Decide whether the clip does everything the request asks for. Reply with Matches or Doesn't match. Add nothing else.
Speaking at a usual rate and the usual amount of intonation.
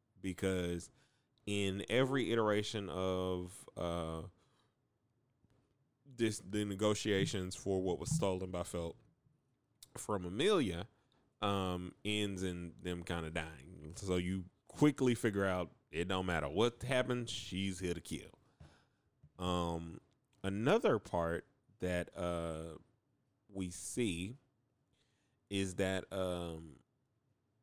Doesn't match